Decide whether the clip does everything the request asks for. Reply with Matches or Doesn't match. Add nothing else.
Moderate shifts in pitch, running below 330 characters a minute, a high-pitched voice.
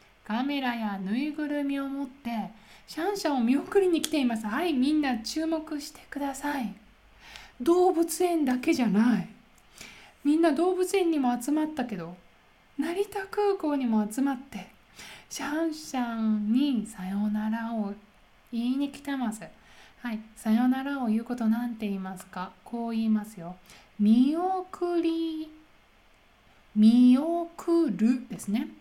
Doesn't match